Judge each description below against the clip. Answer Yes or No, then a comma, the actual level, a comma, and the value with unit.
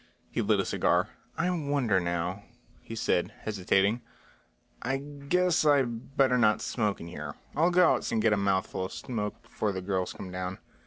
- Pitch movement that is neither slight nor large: No, wide, 6.9 semitones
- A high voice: No, low, 110 Hz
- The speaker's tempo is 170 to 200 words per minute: Yes, average, 175 wpm